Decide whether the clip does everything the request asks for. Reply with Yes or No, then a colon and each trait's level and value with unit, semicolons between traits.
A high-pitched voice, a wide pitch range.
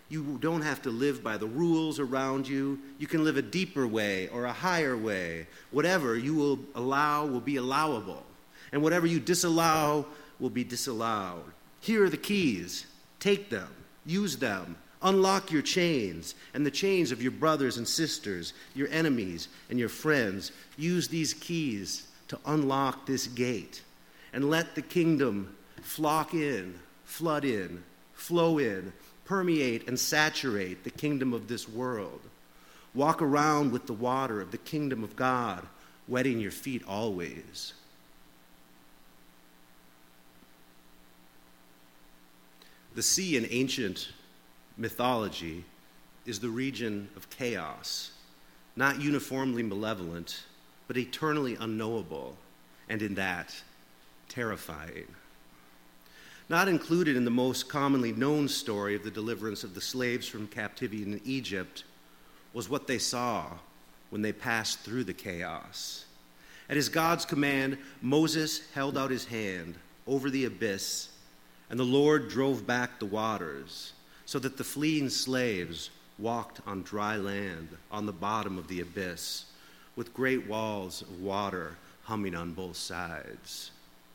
No: low, 115 Hz; wide, 8.6 semitones